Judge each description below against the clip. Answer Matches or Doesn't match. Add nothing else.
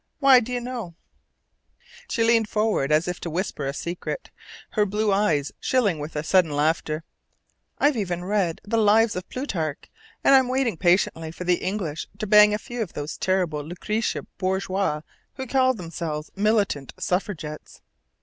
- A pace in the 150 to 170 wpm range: Matches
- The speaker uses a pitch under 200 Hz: Matches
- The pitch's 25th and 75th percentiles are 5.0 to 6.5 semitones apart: Matches